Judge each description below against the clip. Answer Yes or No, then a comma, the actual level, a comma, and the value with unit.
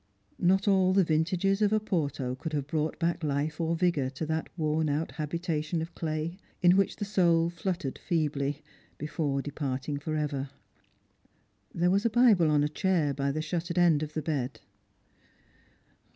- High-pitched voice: No, medium, 160 Hz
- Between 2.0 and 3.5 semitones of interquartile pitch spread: Yes, average, 3.1 semitones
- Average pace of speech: Yes, average, 165 wpm